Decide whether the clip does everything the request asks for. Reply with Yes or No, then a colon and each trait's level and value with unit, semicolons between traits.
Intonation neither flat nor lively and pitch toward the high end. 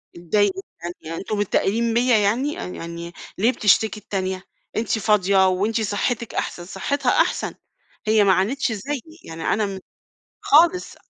Yes: average, 3.6 semitones; high, 205 Hz